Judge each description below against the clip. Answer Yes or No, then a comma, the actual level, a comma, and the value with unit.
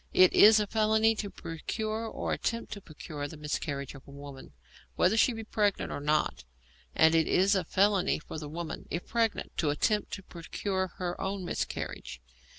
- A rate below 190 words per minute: Yes, average, 180 wpm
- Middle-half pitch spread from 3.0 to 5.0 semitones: No, wide, 5.6 semitones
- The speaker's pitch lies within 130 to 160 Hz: No, medium, 185 Hz